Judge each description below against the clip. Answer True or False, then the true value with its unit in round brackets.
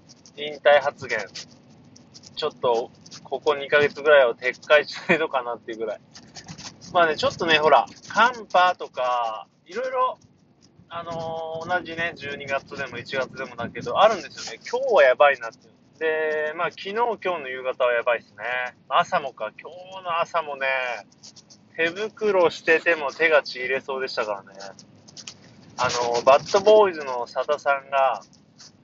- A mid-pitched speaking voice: True (150 Hz)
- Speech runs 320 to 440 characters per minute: False (295 characters per minute)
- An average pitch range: True (4.9 semitones)